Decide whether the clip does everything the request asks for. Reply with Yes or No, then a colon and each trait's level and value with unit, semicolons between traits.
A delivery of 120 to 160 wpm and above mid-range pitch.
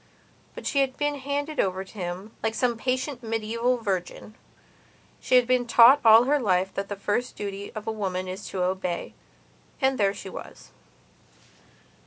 No: average, 170 wpm; high, 220 Hz